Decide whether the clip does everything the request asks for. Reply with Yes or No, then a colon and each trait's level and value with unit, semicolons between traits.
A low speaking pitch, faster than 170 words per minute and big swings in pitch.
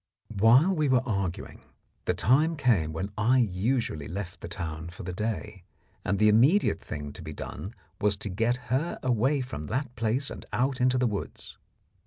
Yes: low, 110 Hz; average, 180 wpm; wide, 5.7 semitones